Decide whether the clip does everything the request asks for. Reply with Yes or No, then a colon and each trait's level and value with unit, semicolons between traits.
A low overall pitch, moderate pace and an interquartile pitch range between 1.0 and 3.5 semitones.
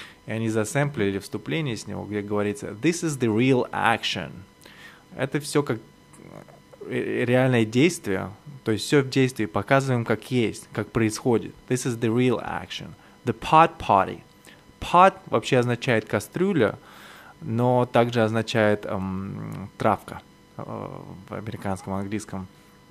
No: low, 115 Hz; average, 130 wpm; average, 3.9 semitones